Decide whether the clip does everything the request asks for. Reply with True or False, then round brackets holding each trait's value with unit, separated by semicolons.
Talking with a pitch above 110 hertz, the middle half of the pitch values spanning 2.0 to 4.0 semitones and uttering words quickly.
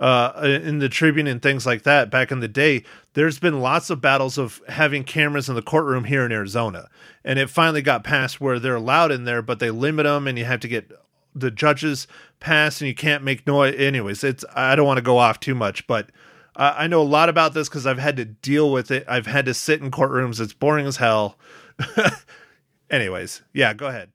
True (135 Hz; 2.8 semitones; 230 wpm)